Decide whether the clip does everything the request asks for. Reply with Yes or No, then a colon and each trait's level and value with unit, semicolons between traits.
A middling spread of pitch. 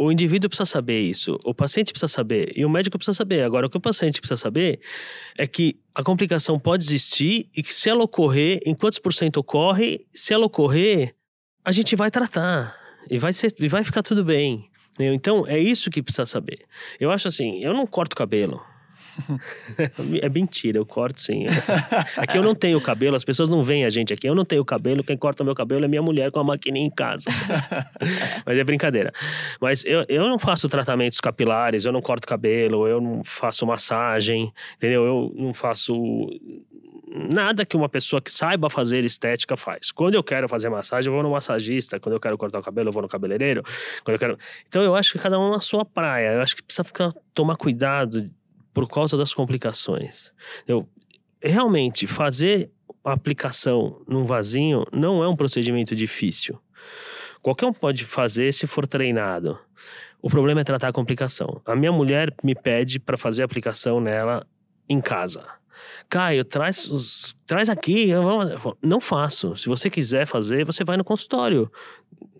No: wide, 6.3 semitones